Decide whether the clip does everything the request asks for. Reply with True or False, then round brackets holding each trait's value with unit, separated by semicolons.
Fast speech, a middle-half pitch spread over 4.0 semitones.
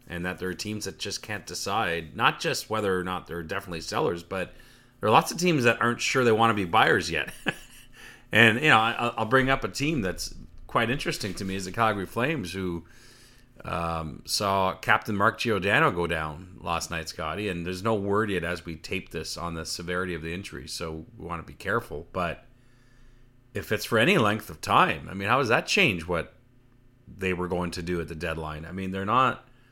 True (220 wpm; 5.2 semitones)